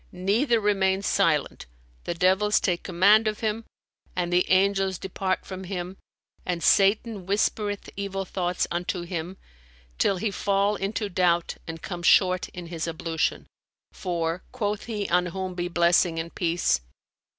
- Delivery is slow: No, average, 145 wpm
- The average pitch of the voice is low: No, medium, 185 Hz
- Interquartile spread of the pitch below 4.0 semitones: Yes, narrow, 2.5 semitones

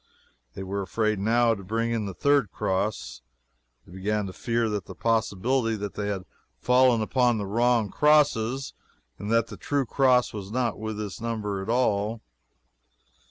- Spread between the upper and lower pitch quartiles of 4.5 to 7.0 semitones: No, average, 2.9 semitones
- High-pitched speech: No, low, 110 Hz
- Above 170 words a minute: No, average, 160 wpm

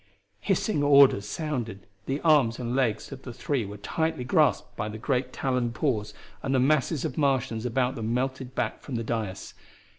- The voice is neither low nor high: No, low, 125 Hz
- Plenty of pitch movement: No, average, 3.3 semitones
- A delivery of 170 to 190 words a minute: Yes, average, 175 wpm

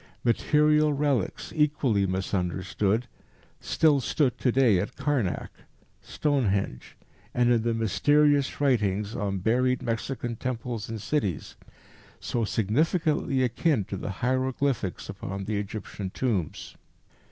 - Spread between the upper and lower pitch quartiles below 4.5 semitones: No, wide, 5.5 semitones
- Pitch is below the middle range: Yes, low, 120 Hz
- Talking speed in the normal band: No, slow, 110 wpm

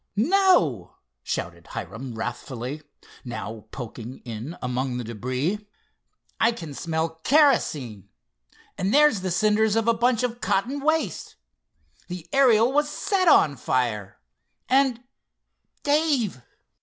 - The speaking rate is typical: No, slow, 110 wpm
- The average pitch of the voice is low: No, medium, 180 Hz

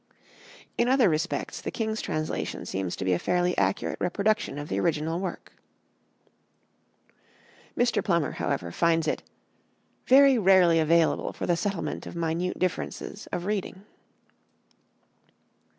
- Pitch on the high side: No, medium, 175 Hz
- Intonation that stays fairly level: No, average, 4.2 semitones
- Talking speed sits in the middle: No, slow, 125 wpm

